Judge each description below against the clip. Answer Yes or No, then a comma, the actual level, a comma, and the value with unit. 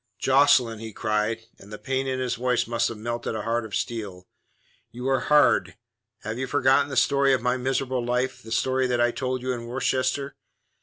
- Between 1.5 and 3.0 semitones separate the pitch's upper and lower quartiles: Yes, narrow, 2.5 semitones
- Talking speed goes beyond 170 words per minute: Yes, average, 200 wpm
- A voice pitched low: Yes, low, 125 Hz